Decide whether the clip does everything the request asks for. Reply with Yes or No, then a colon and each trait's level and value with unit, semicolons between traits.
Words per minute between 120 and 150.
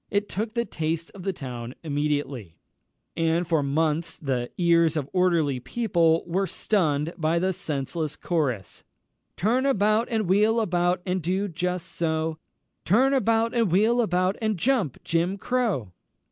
Yes: average, 145 wpm